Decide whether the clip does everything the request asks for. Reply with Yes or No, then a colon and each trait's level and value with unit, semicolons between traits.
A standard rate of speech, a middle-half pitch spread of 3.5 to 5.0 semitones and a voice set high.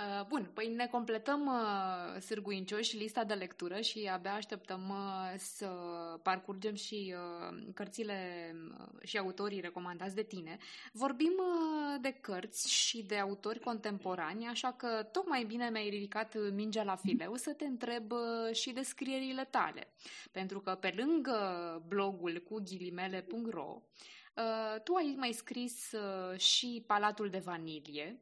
Yes: average, 125 wpm; average, 4.1 semitones; high, 215 Hz